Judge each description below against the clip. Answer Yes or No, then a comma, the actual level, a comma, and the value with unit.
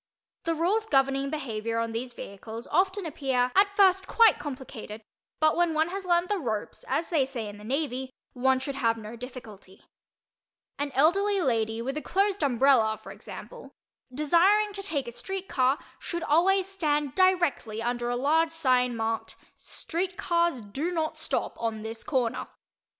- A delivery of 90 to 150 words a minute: No, average, 165 wpm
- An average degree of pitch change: No, wide, 6.5 semitones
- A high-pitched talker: Yes, very high, 275 Hz